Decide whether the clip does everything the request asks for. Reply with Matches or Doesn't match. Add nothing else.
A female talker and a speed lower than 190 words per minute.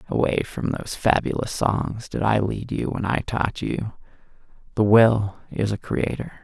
Doesn't match